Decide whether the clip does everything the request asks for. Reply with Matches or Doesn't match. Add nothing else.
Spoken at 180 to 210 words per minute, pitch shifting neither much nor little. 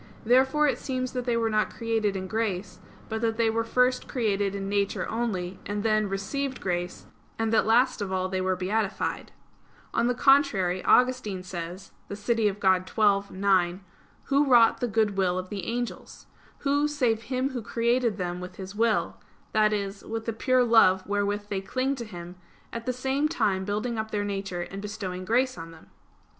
Matches